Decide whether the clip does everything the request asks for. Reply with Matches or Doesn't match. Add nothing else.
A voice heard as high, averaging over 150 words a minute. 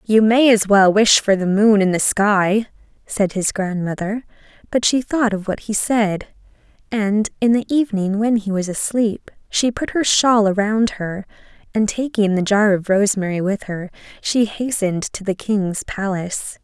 Matches